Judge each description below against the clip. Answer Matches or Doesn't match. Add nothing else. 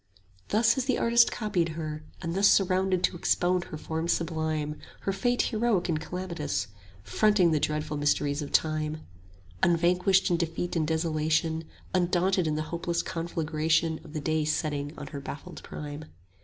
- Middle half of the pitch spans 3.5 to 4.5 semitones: Doesn't match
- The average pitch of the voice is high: Doesn't match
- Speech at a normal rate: Matches